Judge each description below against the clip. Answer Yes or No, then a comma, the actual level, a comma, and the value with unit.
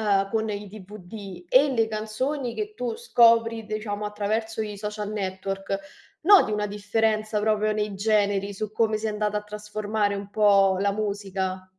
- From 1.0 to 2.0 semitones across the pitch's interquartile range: Yes, narrow, 1.5 semitones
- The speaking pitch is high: Yes, high, 210 Hz